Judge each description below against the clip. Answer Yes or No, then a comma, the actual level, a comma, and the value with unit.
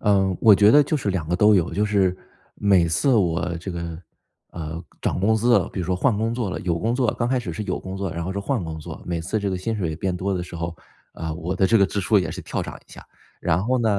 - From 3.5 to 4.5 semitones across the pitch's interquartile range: Yes, average, 3.9 semitones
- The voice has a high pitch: No, very low, 95 Hz